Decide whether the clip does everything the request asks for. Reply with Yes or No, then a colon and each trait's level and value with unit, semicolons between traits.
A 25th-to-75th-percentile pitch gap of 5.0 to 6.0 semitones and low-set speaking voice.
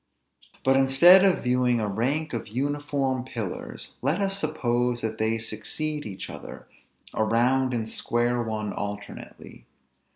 No: average, 4.2 semitones; low, 125 Hz